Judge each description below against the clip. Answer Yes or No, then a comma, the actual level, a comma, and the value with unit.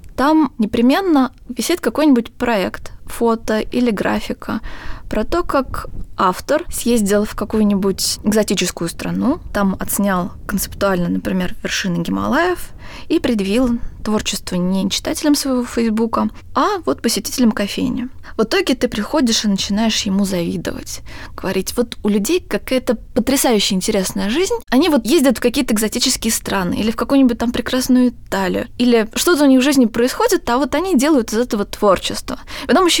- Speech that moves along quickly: No, average, 145 wpm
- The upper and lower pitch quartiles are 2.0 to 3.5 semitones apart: No, average, 4.7 semitones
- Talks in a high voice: Yes, high, 235 Hz